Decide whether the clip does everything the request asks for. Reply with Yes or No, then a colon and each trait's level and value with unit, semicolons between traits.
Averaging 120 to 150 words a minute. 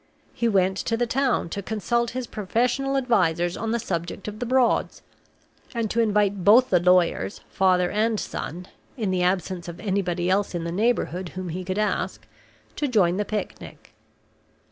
No: average, 170 wpm